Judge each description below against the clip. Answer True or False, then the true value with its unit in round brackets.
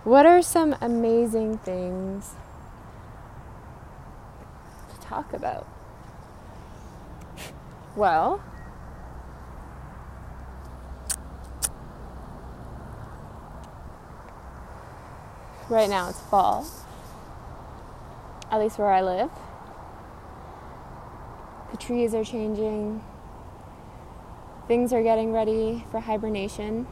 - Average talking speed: False (60 wpm)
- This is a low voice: False (190 Hz)